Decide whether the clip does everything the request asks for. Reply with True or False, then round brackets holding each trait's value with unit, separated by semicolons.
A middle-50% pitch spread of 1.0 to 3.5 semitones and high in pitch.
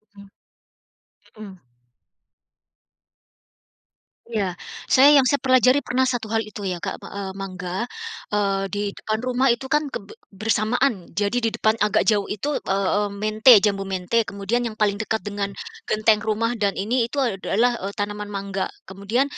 True (3.2 semitones; 215 Hz)